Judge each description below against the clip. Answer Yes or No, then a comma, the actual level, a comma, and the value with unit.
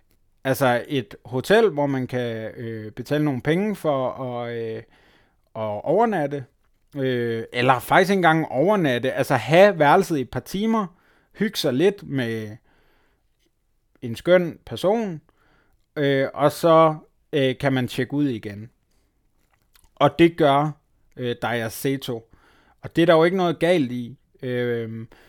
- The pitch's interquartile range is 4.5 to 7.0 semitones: Yes, average, 5.1 semitones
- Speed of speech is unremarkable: No, slow, 140 wpm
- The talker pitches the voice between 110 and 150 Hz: Yes, low, 135 Hz